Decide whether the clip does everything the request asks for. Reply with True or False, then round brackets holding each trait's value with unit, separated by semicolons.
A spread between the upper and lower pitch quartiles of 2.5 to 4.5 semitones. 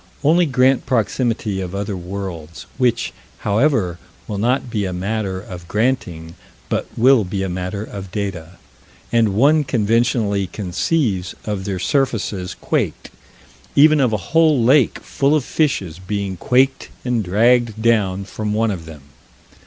False (4.9 semitones)